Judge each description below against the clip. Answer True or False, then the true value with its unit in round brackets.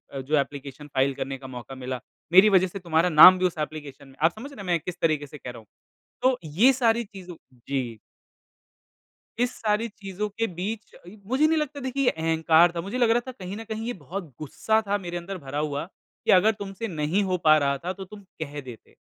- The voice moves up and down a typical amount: False (6.3 semitones)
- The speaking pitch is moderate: True (180 Hz)